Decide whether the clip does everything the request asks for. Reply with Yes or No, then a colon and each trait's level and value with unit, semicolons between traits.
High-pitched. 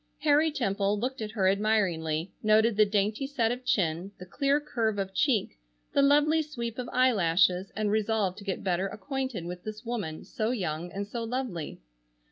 Yes: high, 215 Hz